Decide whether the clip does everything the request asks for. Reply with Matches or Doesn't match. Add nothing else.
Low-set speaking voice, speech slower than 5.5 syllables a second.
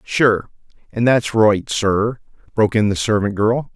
Matches